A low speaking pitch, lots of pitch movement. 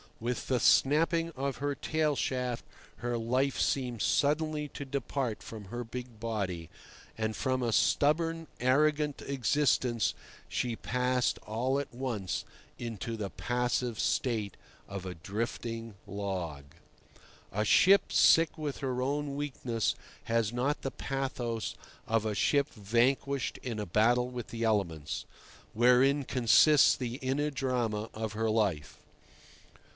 No: low, 125 Hz; average, 3.8 semitones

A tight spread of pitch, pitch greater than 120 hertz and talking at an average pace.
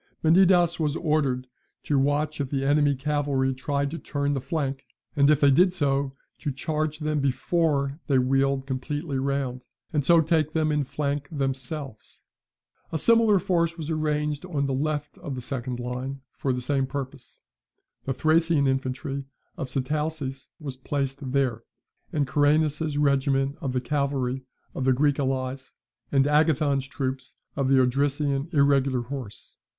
Yes: narrow, 2.2 semitones; medium, 140 Hz; average, 155 wpm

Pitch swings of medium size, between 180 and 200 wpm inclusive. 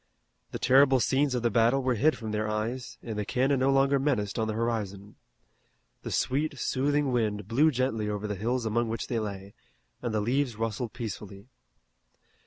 Yes: average, 3.7 semitones; average, 185 wpm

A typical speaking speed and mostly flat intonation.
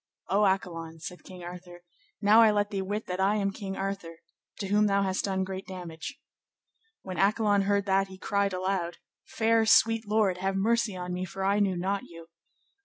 Yes: average, 190 wpm; narrow, 2.0 semitones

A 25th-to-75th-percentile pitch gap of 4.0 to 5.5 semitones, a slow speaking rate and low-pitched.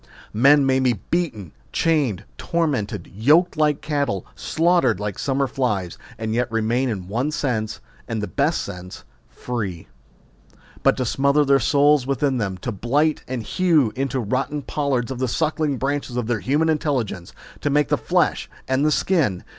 No: average, 4.9 semitones; average, 155 wpm; low, 130 Hz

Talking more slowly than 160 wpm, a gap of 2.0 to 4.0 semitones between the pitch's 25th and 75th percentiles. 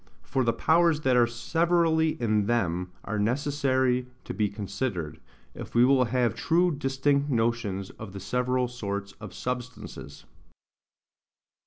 No: slow, 135 wpm; average, 4.6 semitones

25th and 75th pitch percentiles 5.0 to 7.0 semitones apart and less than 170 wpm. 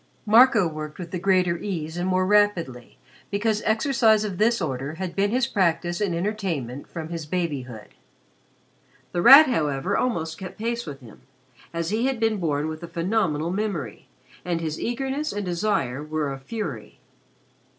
Yes: wide, 5.4 semitones; average, 160 wpm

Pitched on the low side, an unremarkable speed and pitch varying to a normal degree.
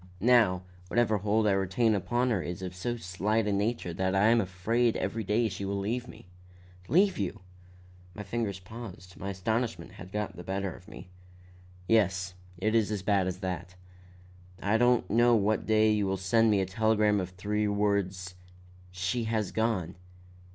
Yes: low, 105 Hz; average, 180 wpm; average, 3.1 semitones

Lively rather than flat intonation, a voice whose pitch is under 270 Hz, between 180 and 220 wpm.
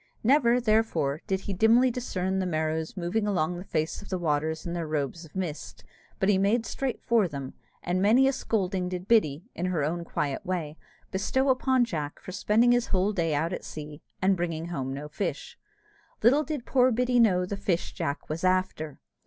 Yes: wide, 5.8 semitones; medium, 185 Hz; average, 195 wpm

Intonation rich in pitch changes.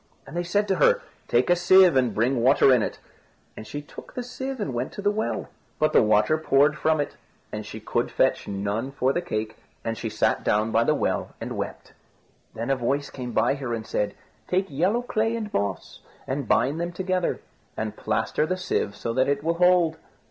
Yes: wide, 7.2 semitones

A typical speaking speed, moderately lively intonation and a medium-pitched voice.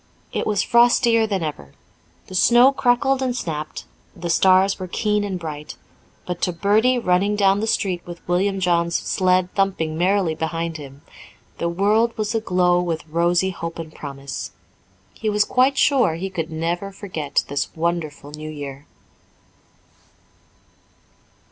Yes: average, 145 wpm; average, 4.2 semitones; medium, 180 Hz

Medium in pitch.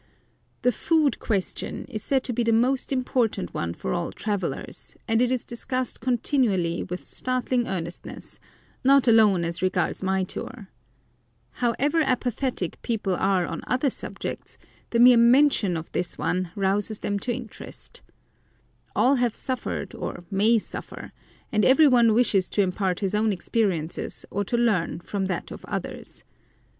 No: high, 225 Hz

